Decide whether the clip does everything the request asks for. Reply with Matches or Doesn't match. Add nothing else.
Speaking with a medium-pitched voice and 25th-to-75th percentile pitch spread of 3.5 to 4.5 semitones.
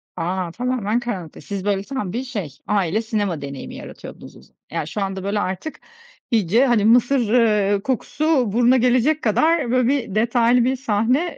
Doesn't match